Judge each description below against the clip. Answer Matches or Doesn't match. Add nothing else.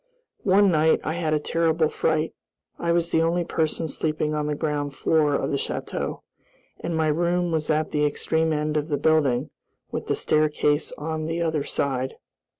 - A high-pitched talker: Doesn't match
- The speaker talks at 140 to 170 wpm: Doesn't match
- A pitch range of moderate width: Doesn't match